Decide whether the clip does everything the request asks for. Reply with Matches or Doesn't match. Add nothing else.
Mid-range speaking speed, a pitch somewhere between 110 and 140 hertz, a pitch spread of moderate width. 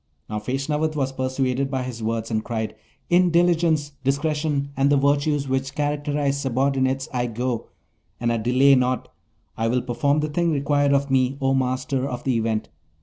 Doesn't match